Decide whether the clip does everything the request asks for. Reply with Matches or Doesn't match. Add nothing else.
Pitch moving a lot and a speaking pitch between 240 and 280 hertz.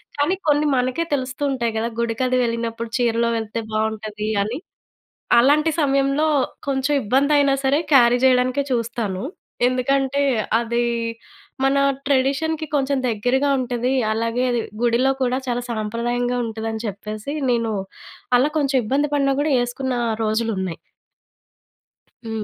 Doesn't match